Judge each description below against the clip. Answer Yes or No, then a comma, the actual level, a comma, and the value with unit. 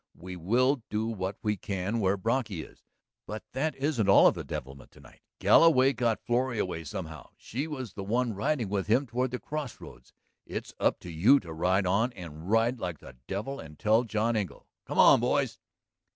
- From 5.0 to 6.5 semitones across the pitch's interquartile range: Yes, average, 5.3 semitones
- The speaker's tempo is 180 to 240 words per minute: Yes, average, 195 wpm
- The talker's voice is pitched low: Yes, low, 110 Hz